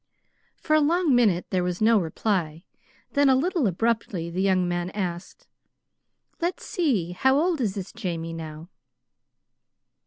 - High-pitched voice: Yes, high, 195 Hz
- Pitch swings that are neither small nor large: No, wide, 7.3 semitones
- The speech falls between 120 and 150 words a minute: Yes, average, 145 wpm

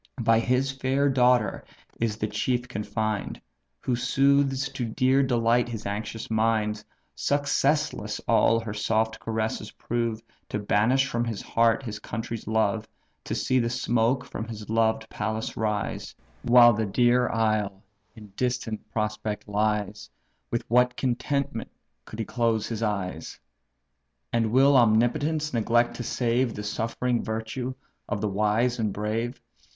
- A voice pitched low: Yes, low, 115 Hz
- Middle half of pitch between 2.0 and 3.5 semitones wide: Yes, narrow, 2.5 semitones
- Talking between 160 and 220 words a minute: No, average, 140 wpm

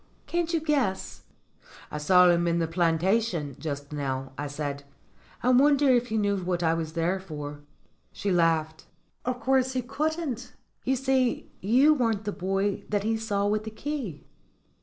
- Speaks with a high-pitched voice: Yes, high, 200 Hz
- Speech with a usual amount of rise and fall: No, wide, 7.4 semitones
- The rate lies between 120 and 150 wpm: No, average, 165 wpm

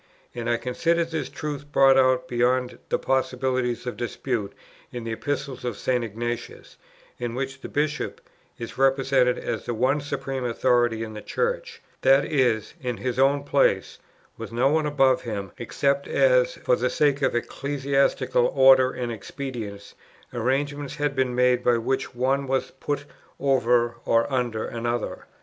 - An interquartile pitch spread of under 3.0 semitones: Yes, narrow, 2.6 semitones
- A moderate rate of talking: Yes, average, 155 wpm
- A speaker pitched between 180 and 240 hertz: No, low, 130 Hz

